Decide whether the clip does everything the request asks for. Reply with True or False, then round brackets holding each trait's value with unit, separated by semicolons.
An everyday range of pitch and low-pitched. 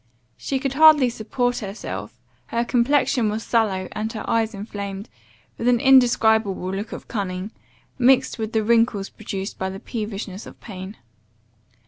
False (3.4 semitones; 220 Hz)